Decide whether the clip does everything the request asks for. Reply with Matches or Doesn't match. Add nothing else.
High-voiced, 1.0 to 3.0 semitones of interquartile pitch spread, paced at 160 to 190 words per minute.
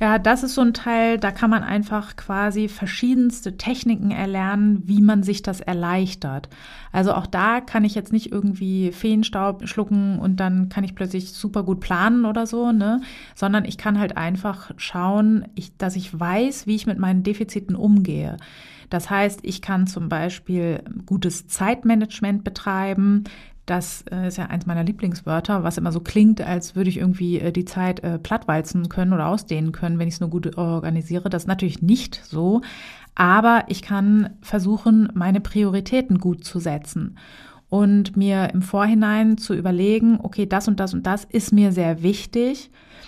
Matches